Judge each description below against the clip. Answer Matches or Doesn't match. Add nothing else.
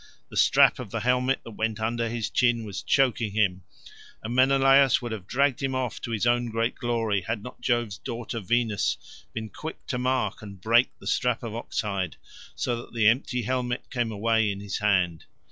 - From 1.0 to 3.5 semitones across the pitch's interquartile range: Matches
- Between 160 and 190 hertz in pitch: Doesn't match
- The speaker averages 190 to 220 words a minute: Matches